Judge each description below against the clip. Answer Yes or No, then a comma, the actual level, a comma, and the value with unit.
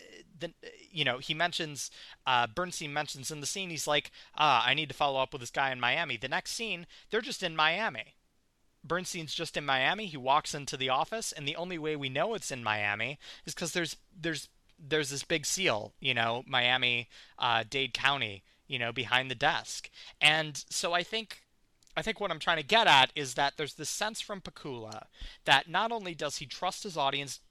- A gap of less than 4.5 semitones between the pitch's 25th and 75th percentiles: No, average, 4.8 semitones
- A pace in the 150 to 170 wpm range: No, fast, 205 wpm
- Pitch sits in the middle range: Yes, medium, 150 Hz